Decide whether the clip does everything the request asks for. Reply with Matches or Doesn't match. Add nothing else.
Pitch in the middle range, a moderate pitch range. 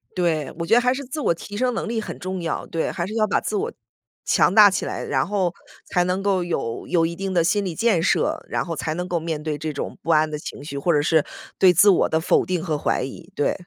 Matches